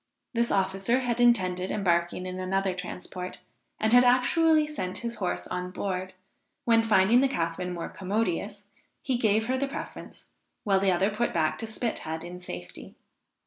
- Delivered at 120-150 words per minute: No, average, 160 wpm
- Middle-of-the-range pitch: No, high, 195 Hz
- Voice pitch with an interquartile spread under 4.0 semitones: No, average, 4.5 semitones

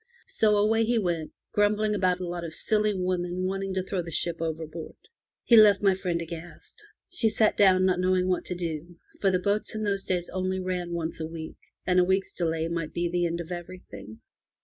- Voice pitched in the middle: Yes, medium, 180 Hz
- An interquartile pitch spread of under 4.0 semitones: Yes, narrow, 2.6 semitones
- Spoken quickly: Yes, fast, 215 wpm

